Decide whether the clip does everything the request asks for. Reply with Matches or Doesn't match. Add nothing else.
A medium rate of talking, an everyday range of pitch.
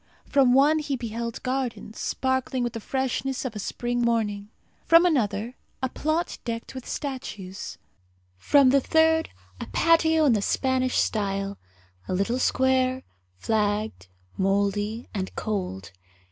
Doesn't match